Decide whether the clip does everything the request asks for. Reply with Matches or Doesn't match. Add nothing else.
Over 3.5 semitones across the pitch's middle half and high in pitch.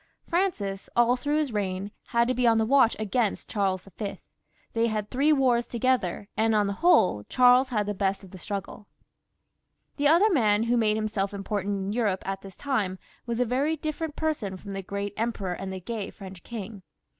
Matches